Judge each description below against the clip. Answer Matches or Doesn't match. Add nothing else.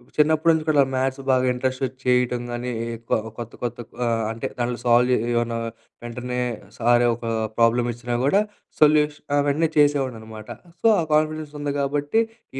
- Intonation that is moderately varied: Matches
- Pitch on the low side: Matches